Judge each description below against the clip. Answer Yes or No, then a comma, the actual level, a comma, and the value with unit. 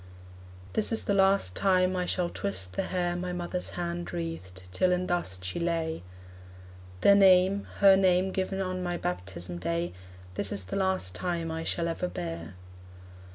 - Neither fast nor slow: Yes, average, 165 wpm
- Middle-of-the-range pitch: Yes, medium, 175 Hz